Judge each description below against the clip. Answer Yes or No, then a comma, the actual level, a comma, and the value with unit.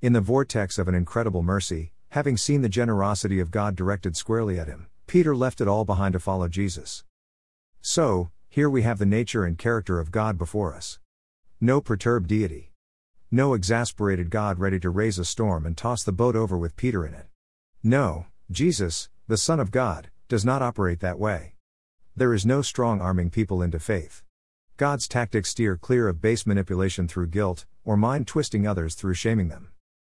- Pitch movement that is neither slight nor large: Yes, average, 4.7 semitones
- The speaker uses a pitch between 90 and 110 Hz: Yes, low, 100 Hz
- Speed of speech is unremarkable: Yes, average, 185 wpm